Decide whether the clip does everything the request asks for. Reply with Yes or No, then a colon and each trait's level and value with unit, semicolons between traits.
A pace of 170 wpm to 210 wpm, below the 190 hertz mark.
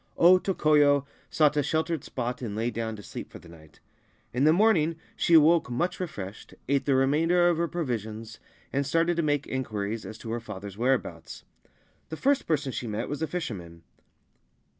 Yes: average, 180 wpm; medium, 140 Hz